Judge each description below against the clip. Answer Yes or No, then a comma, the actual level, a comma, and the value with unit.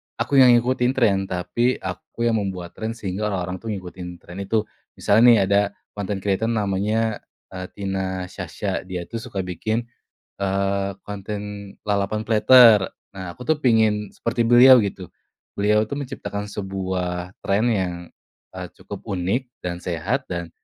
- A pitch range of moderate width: Yes, average, 3.2 semitones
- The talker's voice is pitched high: No, low, 100 Hz